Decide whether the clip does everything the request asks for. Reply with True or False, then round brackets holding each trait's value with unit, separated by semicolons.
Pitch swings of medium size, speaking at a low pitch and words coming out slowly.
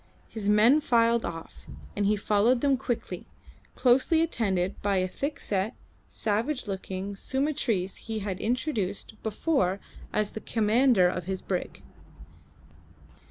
False (4.3 semitones; 215 Hz; 125 wpm)